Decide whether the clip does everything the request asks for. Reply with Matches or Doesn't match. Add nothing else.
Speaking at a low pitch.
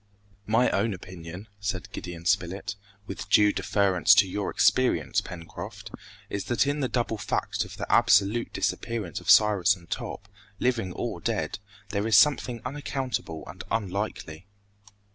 Matches